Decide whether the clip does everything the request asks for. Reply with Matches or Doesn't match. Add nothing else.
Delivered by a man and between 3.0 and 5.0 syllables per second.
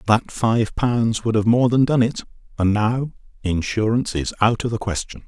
Matches